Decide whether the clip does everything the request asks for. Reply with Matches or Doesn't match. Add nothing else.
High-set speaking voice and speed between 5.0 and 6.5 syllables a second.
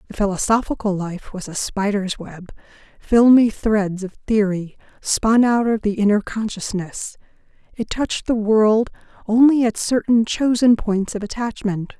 Doesn't match